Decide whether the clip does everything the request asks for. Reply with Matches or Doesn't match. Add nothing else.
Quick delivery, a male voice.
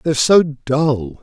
Doesn't match